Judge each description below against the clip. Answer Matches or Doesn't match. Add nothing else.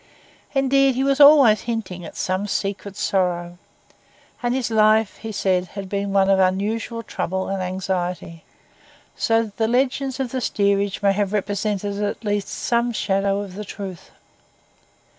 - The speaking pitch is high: Matches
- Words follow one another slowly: Doesn't match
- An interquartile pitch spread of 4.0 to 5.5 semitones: Doesn't match